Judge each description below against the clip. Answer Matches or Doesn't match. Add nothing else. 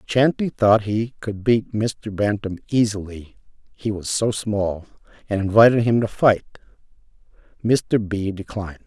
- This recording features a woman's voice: Doesn't match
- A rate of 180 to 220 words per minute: Doesn't match